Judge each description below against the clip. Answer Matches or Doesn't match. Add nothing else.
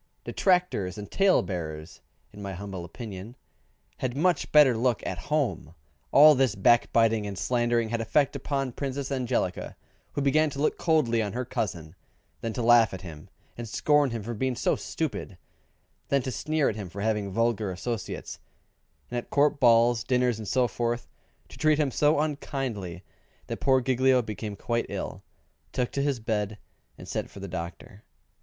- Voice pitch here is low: Matches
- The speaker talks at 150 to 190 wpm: Matches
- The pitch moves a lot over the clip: Doesn't match